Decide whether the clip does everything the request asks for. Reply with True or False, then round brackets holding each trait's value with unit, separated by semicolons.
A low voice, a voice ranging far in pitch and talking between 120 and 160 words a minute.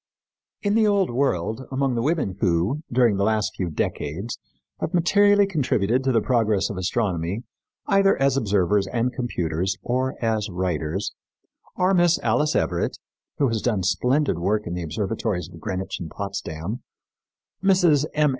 True (110 Hz; 6.6 semitones; 155 wpm)